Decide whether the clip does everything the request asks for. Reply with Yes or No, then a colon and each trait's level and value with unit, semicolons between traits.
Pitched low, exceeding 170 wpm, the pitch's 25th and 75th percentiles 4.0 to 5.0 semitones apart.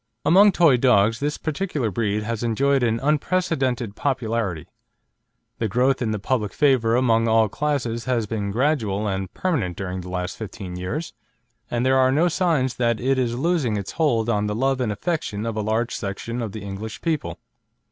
Yes: low, 115 Hz; average, 180 wpm; average, 4.5 semitones